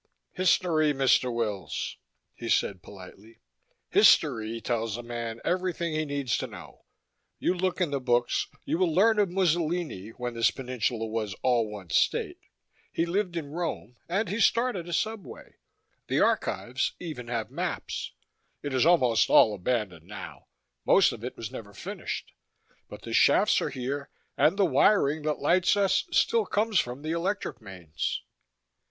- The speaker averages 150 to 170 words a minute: Yes, average, 160 wpm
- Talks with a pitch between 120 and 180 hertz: Yes, medium, 140 Hz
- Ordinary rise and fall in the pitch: No, wide, 7.3 semitones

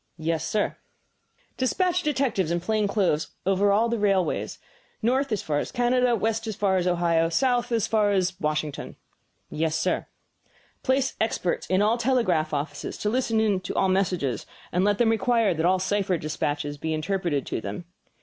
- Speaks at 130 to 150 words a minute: No, average, 170 wpm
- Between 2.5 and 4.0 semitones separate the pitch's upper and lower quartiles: No, wide, 5.5 semitones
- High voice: Yes, high, 195 Hz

